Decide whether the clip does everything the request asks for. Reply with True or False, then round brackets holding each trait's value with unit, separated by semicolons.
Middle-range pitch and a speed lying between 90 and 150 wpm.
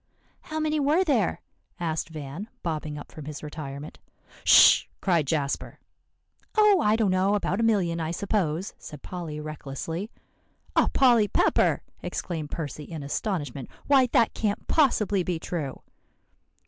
True (175 Hz; 140 wpm)